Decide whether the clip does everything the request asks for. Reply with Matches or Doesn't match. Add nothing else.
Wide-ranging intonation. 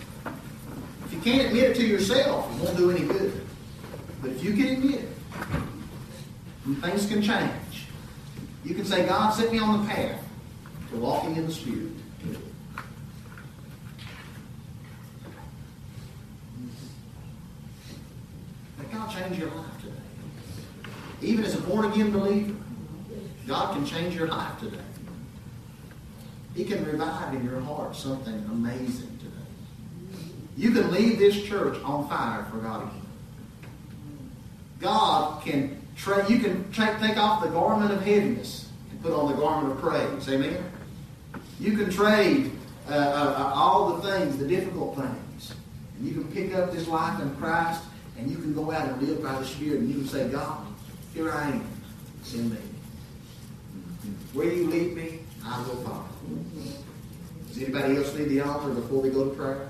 Matches